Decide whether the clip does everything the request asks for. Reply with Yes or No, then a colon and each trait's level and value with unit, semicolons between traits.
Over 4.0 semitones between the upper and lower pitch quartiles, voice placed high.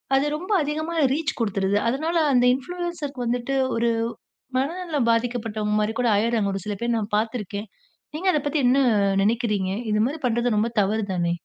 Yes: average, 5.1 semitones; high, 235 Hz